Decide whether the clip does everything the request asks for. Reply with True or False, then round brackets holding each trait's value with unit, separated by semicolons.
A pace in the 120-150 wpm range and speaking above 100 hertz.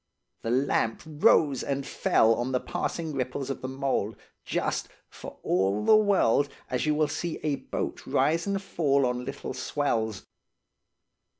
True (140 wpm; 135 Hz)